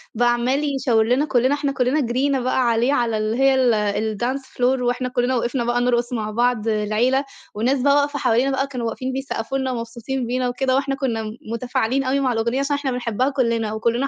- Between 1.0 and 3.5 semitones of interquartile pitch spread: Yes, narrow, 2.5 semitones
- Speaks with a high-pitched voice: Yes, very high, 250 Hz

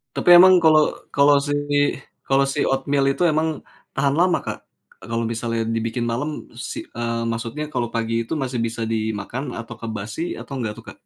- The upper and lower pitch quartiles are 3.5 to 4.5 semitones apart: Yes, average, 3.9 semitones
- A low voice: Yes, low, 120 Hz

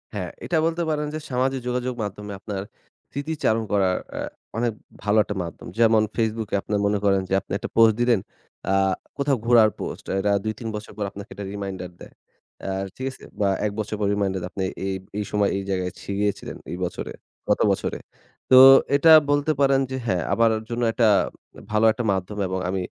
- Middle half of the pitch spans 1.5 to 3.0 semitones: No, average, 3.7 semitones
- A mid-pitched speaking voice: No, low, 105 Hz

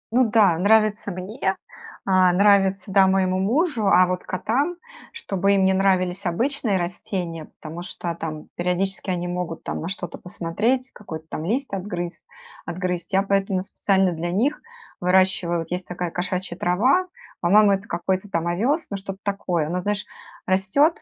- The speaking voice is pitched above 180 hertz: Yes, high, 190 Hz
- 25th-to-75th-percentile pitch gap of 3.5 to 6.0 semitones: No, narrow, 2.5 semitones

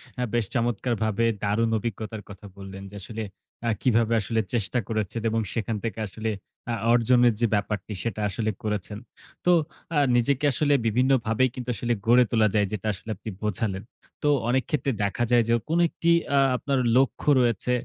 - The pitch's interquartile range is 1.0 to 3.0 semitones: Yes, narrow, 2.5 semitones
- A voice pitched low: Yes, low, 115 Hz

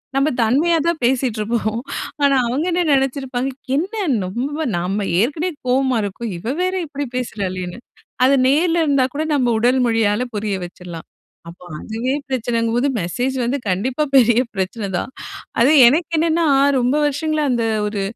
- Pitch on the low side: No, very high, 250 Hz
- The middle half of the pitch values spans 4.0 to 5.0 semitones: Yes, average, 4.6 semitones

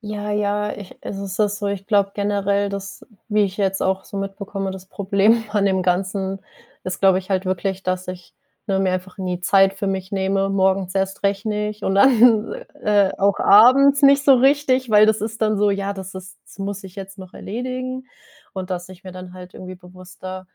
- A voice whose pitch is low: No, high, 195 Hz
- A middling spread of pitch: No, narrow, 1.8 semitones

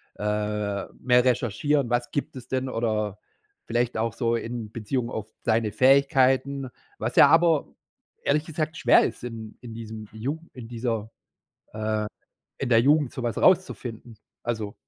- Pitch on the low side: Yes, low, 120 Hz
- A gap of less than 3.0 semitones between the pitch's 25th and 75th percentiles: No, average, 3.3 semitones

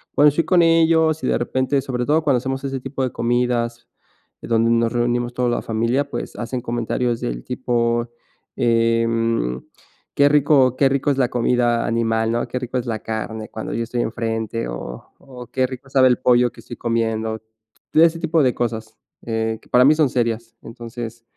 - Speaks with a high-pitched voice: No, low, 120 Hz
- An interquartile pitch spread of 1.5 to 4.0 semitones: Yes, narrow, 2.4 semitones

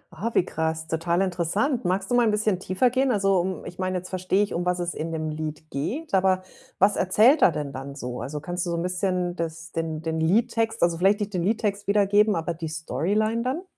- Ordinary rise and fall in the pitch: Yes, average, 4.1 semitones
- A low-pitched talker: No, medium, 185 Hz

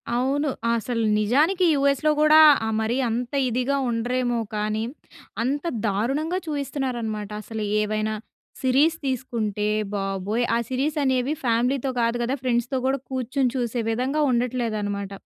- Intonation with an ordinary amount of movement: Yes, average, 3.5 semitones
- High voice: Yes, high, 245 Hz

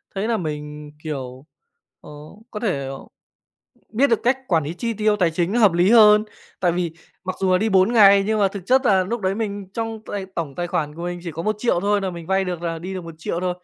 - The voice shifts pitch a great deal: No, average, 3.9 semitones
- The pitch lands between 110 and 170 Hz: No, medium, 185 Hz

